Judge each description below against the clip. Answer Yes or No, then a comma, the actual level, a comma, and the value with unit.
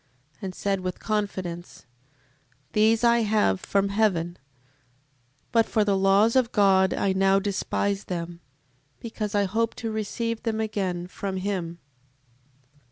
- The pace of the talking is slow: Yes, slow, 130 wpm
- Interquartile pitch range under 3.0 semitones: Yes, narrow, 2.5 semitones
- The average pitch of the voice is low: No, high, 200 Hz